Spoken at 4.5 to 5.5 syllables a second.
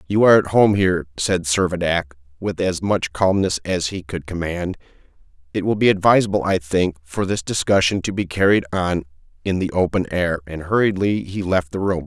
Yes: 5.3 syllables/s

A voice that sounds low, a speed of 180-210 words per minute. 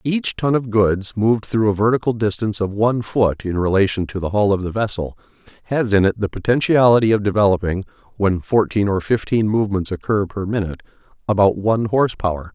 Yes: low, 105 Hz; average, 185 wpm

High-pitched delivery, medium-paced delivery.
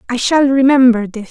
Yes: very high, 250 Hz; average, 185 wpm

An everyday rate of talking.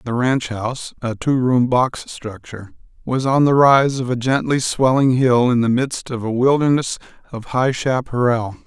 Yes: average, 165 wpm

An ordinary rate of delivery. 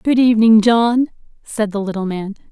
Yes: average, 165 wpm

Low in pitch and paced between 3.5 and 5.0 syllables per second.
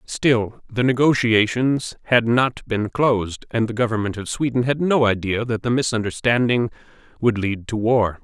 Yes: low, 115 Hz; 4.7 syllables/s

